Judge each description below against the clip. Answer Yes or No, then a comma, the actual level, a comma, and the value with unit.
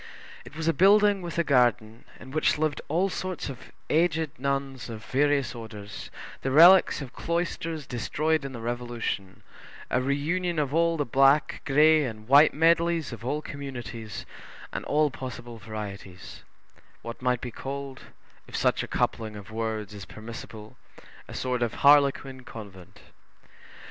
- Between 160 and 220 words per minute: No, average, 150 wpm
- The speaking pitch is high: No, low, 135 Hz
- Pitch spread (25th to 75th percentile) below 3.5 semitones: No, average, 5.2 semitones